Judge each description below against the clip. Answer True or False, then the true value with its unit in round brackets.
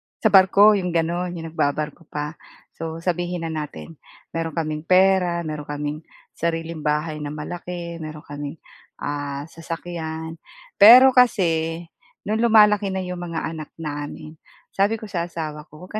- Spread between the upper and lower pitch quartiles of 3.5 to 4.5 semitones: False (2.8 semitones)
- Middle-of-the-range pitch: True (165 Hz)